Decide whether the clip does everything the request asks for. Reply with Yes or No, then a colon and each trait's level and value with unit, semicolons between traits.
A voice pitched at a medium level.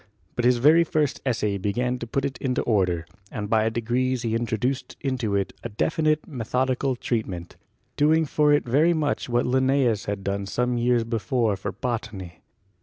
No: low, 120 Hz